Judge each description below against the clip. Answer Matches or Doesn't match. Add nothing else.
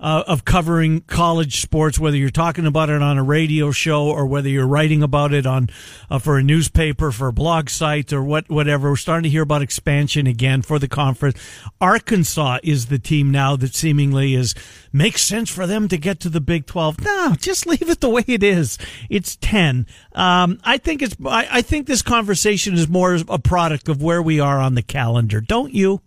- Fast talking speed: Matches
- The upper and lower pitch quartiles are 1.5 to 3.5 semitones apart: Doesn't match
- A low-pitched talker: Doesn't match